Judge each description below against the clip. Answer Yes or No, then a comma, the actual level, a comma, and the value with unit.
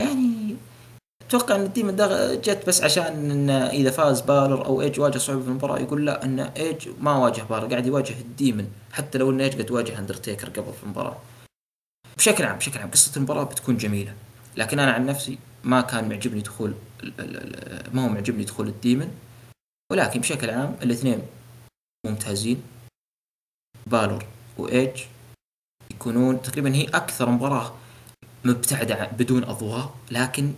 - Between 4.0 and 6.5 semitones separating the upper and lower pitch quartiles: No, average, 3.1 semitones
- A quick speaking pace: Yes, fast, 145 wpm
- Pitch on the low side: Yes, low, 125 Hz